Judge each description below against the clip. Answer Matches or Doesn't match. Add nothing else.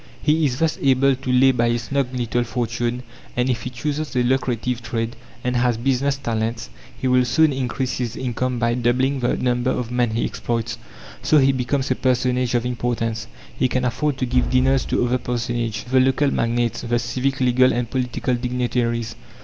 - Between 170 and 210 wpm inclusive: Matches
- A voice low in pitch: Matches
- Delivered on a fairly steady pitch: Matches